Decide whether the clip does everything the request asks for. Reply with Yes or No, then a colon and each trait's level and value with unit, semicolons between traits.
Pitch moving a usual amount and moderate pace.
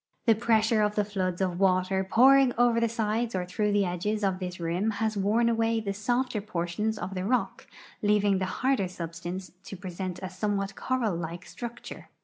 Yes: average, 3.4 semitones; average, 185 wpm